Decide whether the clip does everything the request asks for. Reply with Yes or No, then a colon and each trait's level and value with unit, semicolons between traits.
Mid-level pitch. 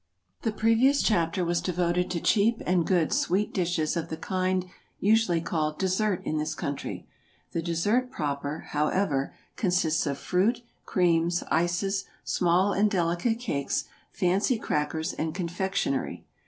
Yes: medium, 180 Hz